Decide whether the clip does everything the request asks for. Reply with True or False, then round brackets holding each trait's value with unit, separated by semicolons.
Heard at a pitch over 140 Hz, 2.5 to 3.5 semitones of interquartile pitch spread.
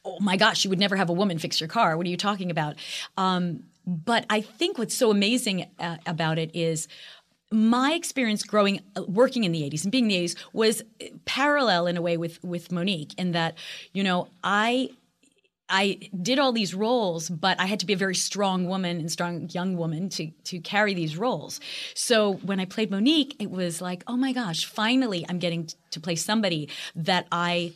False (190 Hz; 3.9 semitones)